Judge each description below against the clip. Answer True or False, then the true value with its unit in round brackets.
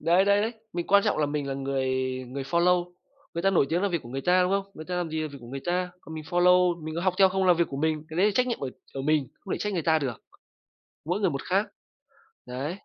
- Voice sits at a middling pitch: True (170 Hz)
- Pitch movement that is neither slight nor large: True (3.9 semitones)